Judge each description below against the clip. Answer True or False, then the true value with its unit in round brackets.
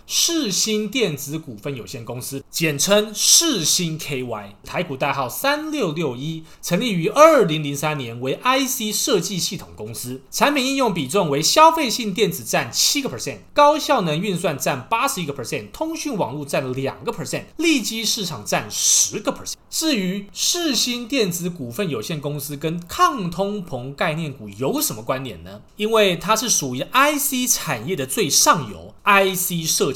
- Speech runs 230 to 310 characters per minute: True (300 characters per minute)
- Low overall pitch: False (180 Hz)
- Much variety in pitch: True (8.5 semitones)